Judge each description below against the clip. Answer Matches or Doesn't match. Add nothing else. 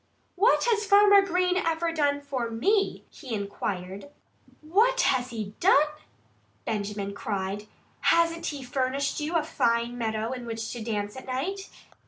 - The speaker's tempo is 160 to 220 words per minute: Doesn't match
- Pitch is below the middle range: Doesn't match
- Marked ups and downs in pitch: Matches